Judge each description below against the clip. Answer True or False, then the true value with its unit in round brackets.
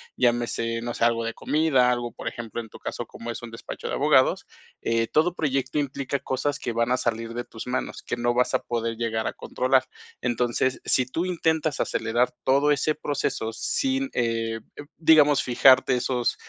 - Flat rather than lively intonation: False (3.3 semitones)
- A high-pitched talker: False (125 Hz)